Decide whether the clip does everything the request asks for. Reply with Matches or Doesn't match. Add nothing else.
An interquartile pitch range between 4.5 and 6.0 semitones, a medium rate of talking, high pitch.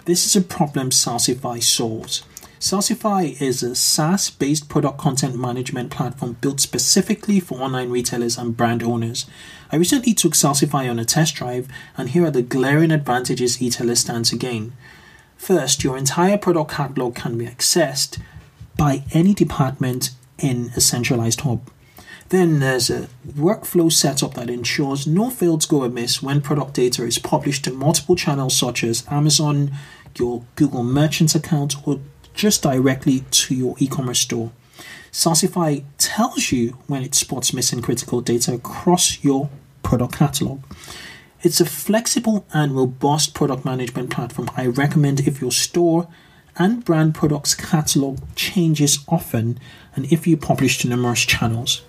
Doesn't match